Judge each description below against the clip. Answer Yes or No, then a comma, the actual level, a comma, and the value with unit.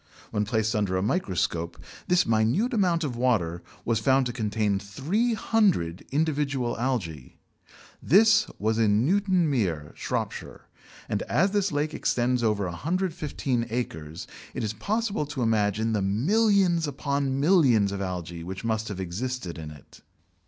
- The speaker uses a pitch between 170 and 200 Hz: No, low, 120 Hz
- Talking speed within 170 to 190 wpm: No, average, 140 wpm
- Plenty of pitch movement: Yes, wide, 7.7 semitones